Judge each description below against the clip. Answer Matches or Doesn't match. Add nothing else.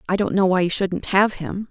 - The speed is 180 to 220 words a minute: Doesn't match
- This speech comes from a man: Doesn't match